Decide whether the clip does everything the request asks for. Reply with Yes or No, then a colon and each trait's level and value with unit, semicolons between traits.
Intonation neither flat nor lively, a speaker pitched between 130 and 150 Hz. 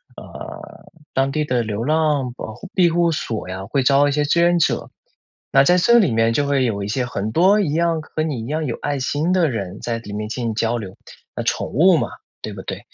No: wide, 5.9 semitones; medium, 140 Hz